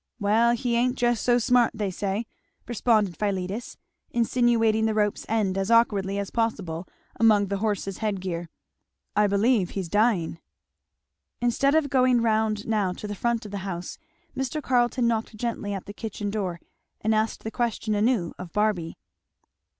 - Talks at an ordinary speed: Yes, average, 160 wpm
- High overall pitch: Yes, high, 215 Hz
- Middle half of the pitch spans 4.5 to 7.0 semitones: No, average, 3.1 semitones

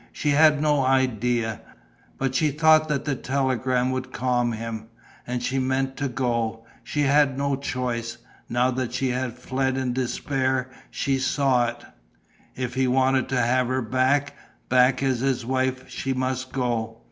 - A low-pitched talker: Yes, low, 130 Hz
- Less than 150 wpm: No, average, 160 wpm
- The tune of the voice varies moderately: No, narrow, 1.4 semitones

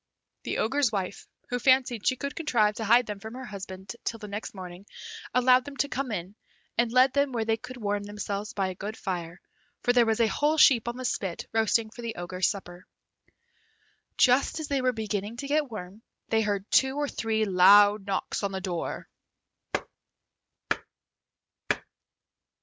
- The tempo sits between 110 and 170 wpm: No, average, 180 wpm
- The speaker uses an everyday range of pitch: Yes, average, 4.0 semitones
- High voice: Yes, high, 220 Hz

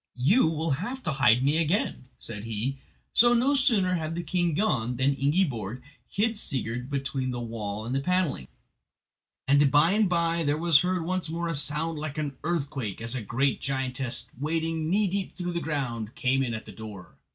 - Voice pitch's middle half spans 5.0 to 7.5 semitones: Yes, average, 5.3 semitones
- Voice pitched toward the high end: No, medium, 145 Hz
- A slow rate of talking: No, average, 190 wpm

